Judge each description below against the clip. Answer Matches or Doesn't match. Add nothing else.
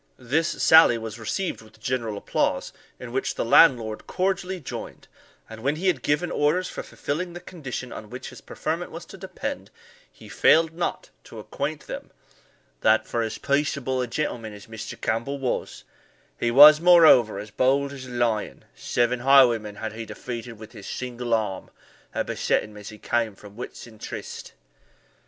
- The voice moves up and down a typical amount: Matches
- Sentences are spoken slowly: Doesn't match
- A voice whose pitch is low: Matches